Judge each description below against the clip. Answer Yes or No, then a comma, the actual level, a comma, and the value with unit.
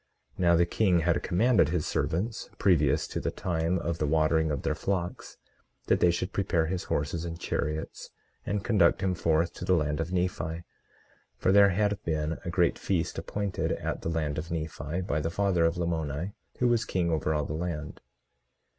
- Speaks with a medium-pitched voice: No, very low, 85 Hz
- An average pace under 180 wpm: No, average, 190 wpm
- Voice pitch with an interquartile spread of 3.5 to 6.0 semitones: No, average, 2.7 semitones